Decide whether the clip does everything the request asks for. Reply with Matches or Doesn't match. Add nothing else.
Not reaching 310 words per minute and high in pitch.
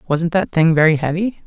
Doesn't match